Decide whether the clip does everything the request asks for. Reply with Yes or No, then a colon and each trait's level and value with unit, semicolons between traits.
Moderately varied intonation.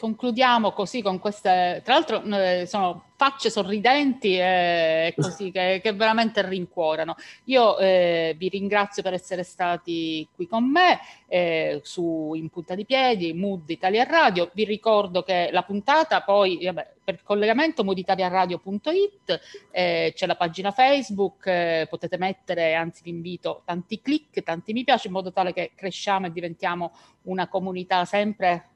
Yes: average, 3.4 semitones